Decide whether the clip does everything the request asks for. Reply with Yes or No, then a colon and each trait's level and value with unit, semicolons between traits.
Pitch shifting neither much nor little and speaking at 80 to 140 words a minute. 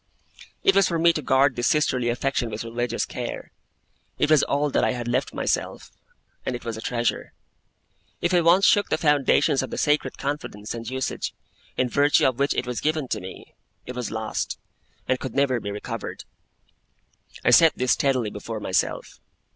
No: average, 3.7 semitones; average, 185 wpm